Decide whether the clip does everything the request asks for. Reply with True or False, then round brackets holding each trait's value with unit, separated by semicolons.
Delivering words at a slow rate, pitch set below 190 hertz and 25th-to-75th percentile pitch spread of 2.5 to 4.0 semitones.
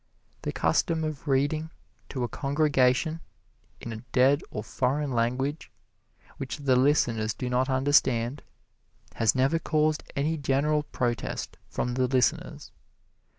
True (125 wpm; 135 Hz; 3.0 semitones)